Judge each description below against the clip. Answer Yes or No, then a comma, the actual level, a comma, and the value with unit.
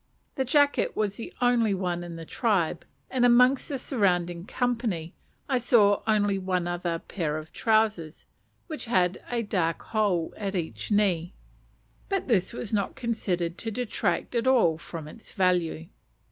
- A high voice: Yes, high, 200 Hz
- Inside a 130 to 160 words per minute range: Yes, average, 155 wpm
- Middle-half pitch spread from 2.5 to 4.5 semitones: No, average, 5.2 semitones